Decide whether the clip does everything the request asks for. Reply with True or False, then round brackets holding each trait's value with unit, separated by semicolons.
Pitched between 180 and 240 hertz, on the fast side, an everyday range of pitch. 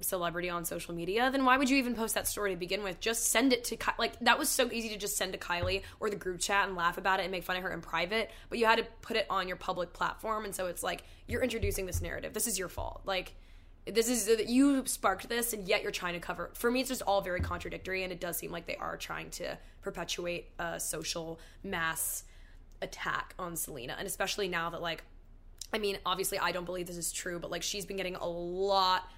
True (190 Hz; 255 wpm; 4.0 semitones)